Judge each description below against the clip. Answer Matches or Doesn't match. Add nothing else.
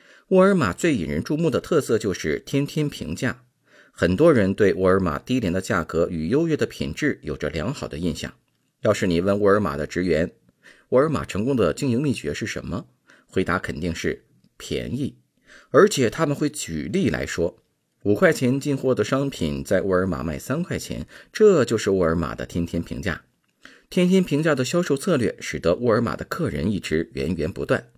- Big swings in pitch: Matches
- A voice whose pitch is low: Matches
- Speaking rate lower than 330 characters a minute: Matches